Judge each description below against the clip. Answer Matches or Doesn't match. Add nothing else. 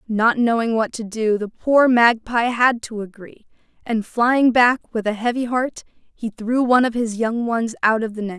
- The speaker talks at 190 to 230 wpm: Matches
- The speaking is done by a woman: Matches